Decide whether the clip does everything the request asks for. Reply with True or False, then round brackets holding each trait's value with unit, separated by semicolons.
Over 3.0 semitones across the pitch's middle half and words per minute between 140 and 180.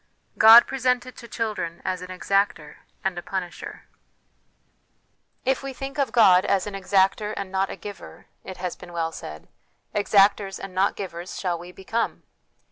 True (3.4 semitones; 170 wpm)